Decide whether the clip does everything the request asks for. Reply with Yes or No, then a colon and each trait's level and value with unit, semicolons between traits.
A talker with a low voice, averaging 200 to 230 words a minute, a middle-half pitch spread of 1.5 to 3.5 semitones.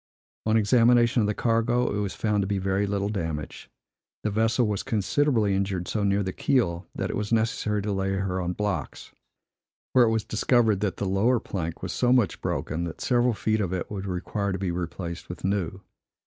Yes: low, 100 Hz; fast, 205 wpm; average, 2.9 semitones